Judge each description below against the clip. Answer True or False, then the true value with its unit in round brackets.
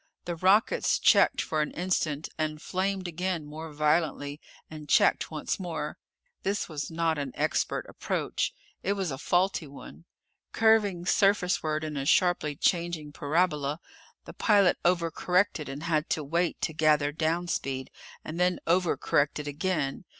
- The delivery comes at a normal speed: True (150 wpm)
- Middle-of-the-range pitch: True (160 Hz)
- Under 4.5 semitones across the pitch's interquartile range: True (3.1 semitones)